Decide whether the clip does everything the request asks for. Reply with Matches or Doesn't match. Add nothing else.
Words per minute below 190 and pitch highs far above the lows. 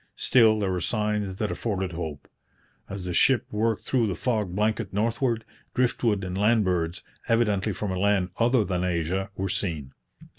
Doesn't match